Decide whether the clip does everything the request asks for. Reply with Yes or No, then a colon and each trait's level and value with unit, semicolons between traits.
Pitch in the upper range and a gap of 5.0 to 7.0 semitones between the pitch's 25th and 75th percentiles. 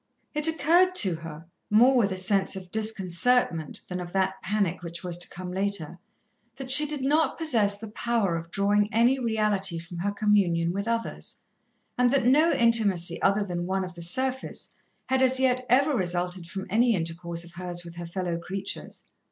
Yes: high, 195 Hz; wide, 5.5 semitones